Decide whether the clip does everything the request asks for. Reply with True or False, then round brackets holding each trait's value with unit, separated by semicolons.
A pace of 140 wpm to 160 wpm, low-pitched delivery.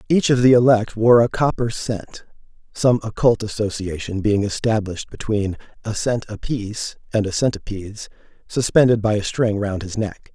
True (155 wpm; 110 Hz)